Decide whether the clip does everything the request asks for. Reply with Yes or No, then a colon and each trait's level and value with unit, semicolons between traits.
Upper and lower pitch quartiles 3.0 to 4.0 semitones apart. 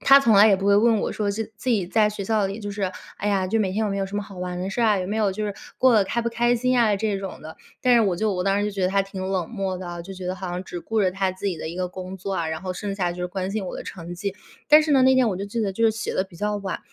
No: narrow, 2.6 semitones